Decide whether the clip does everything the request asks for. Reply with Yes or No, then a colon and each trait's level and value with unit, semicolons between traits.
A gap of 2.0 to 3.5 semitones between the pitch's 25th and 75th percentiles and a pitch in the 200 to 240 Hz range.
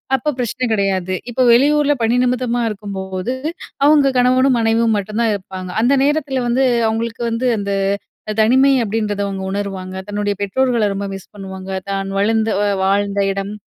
No: average, 4.1 semitones; high, 220 Hz